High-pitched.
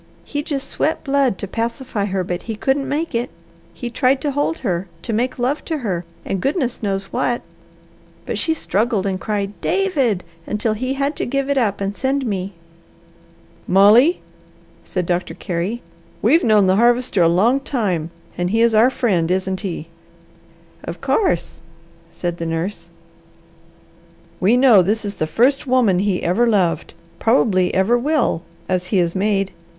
Yes: high, 215 Hz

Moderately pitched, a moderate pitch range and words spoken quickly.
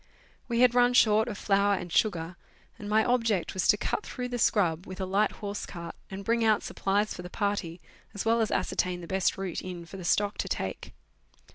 No: high, 200 Hz; average, 3.2 semitones; fast, 220 wpm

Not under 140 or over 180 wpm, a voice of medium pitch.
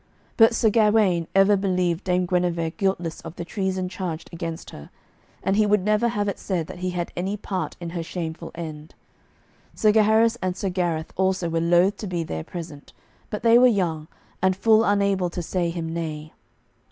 No: average, 190 wpm; medium, 180 Hz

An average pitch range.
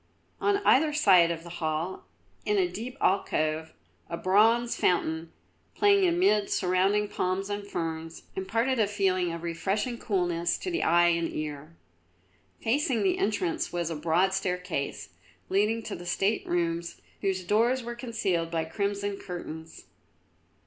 Yes: average, 4.7 semitones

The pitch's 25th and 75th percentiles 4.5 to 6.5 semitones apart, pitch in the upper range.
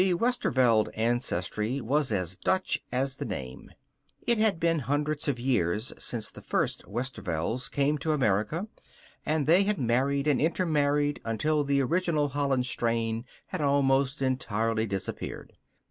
No: average, 4.9 semitones; low, 135 Hz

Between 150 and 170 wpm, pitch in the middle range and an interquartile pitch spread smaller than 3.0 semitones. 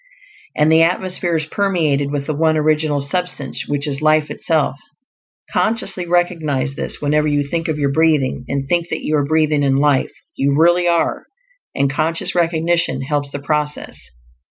Yes: average, 165 wpm; medium, 155 Hz; narrow, 2.6 semitones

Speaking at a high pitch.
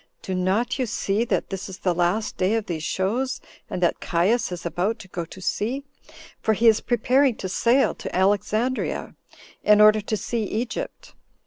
Yes: high, 210 Hz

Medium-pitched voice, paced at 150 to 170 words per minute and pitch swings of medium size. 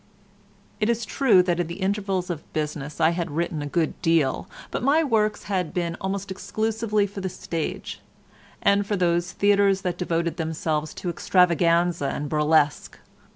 Yes: medium, 175 Hz; average, 160 wpm; average, 3.6 semitones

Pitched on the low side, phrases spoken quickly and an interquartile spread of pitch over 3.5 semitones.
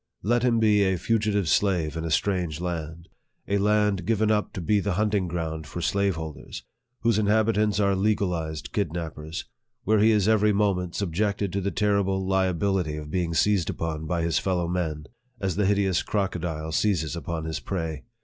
No: very low, 95 Hz; average, 175 wpm; average, 3.9 semitones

